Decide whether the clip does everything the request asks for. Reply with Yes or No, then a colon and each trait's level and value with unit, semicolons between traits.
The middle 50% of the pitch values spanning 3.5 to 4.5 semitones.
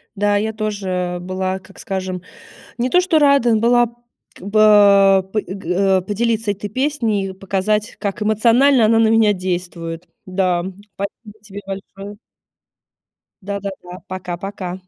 No: average, 2.7 semitones